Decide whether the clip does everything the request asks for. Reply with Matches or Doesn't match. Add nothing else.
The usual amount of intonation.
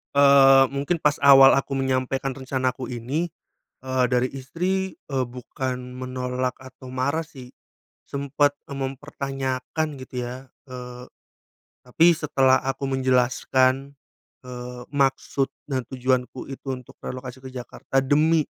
Doesn't match